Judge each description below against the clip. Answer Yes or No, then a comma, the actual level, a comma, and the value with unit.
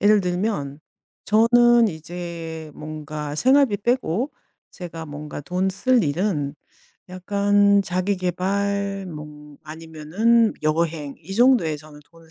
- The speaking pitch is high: No, medium, 180 Hz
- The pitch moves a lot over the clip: No, average, 4.7 semitones